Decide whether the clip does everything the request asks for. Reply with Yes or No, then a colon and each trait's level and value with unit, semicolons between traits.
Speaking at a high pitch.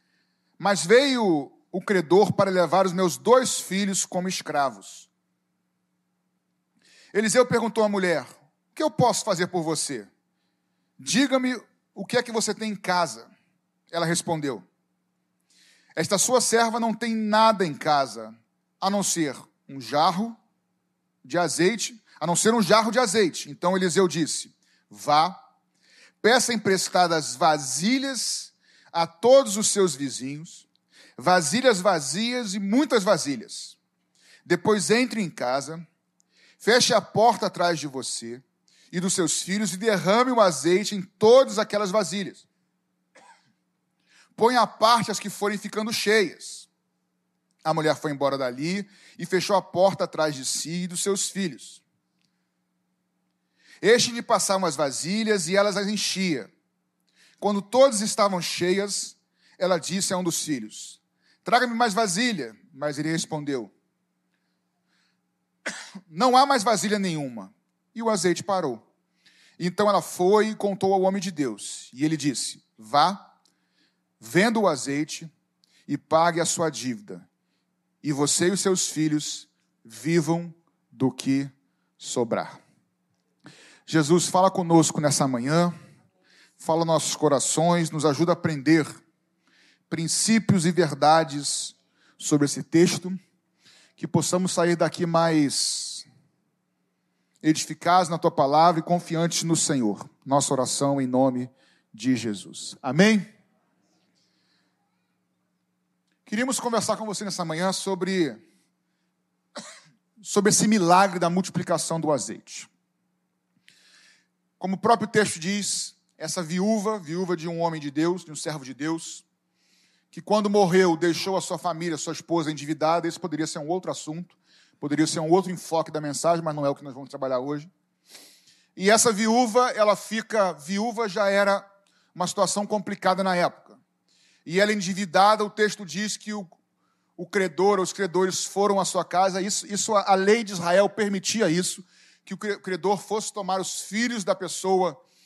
No: medium, 180 Hz